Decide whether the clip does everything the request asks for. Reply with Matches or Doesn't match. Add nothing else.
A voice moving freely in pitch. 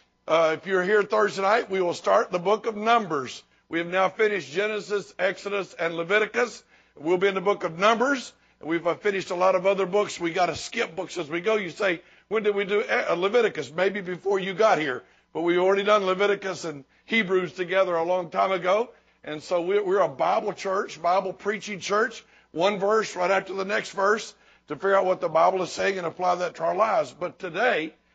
Doesn't match